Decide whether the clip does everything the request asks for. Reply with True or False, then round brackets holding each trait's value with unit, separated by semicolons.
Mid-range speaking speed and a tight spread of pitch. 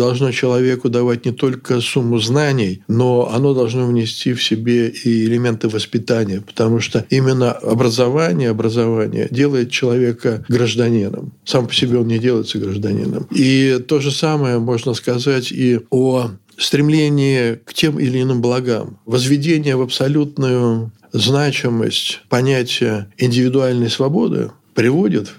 True (125 wpm; 2.2 semitones)